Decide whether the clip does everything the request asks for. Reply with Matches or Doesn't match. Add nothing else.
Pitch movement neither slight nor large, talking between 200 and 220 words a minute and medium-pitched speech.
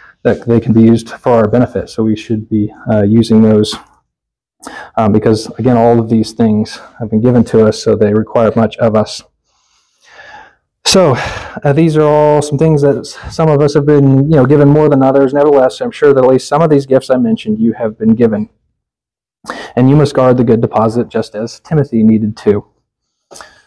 Doesn't match